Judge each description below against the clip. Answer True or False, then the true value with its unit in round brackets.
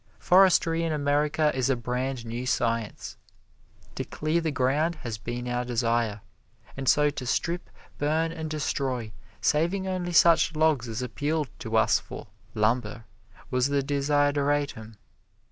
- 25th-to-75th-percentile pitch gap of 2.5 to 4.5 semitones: True (4.2 semitones)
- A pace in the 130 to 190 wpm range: True (140 wpm)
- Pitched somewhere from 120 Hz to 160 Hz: True (140 Hz)